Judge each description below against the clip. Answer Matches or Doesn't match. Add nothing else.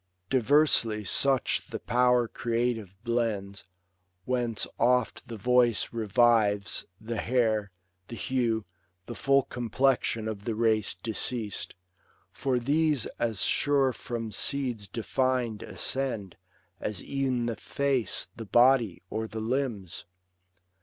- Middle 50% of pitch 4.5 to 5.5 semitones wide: Doesn't match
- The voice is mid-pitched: Doesn't match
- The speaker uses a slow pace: Matches